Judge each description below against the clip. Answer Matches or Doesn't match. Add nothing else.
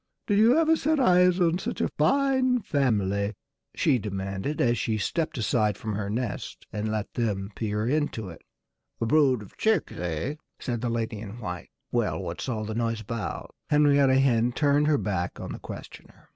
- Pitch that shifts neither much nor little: Doesn't match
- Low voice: Matches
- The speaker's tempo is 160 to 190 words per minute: Matches